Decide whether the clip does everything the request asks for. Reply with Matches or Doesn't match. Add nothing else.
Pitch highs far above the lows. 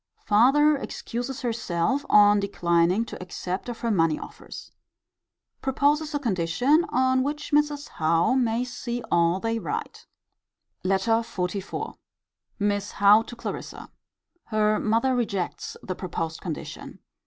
Matches